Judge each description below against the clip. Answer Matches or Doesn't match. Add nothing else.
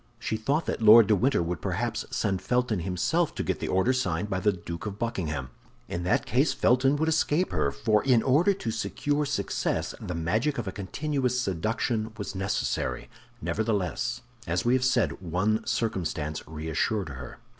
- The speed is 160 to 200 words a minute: Matches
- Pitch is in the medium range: Doesn't match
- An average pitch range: Doesn't match